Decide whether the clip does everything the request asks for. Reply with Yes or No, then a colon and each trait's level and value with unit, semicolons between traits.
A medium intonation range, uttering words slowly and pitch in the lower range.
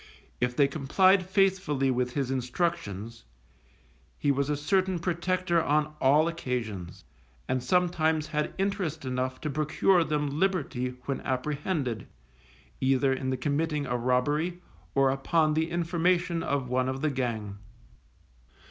No: average, 4.7 semitones; slow, 130 wpm; medium, 145 Hz